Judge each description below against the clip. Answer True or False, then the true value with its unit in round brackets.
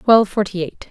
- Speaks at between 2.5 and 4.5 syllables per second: False (5.8 syllables/s)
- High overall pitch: True (200 Hz)